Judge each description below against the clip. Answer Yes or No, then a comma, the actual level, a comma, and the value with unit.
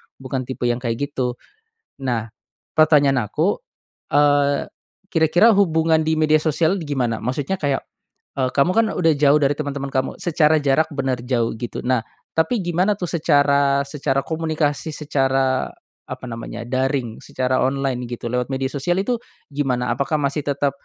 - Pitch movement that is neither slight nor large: Yes, average, 3.2 semitones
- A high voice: No, medium, 140 Hz